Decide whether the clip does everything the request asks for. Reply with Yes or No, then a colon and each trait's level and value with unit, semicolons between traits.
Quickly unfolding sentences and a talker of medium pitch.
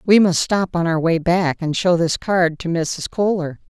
Yes: fast, 225 wpm; medium, 175 Hz